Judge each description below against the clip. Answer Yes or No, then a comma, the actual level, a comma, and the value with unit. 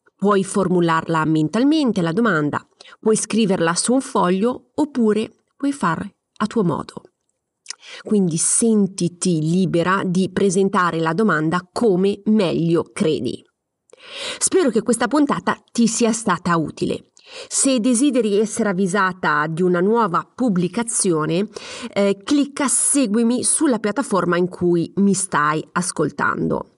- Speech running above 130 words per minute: No, slow, 115 wpm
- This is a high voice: Yes, high, 200 Hz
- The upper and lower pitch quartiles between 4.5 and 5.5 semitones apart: Yes, average, 5.1 semitones